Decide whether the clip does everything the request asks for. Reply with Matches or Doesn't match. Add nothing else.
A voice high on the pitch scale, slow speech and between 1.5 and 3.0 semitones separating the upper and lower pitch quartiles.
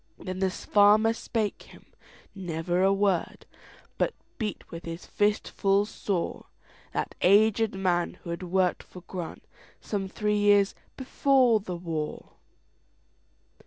Matches